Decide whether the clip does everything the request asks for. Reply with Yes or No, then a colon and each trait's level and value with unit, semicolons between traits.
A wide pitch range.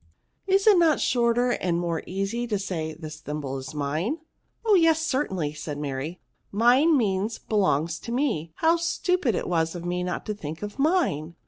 Yes: wide, 8.8 semitones